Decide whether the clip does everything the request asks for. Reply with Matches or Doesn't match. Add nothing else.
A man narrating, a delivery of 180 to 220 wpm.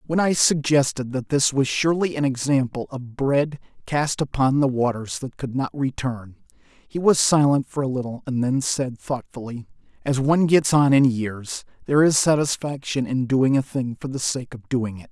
Matches